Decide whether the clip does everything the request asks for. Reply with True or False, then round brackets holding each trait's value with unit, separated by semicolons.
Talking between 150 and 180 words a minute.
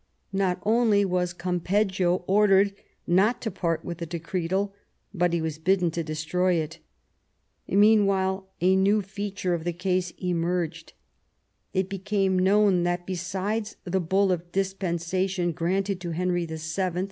False (140 wpm)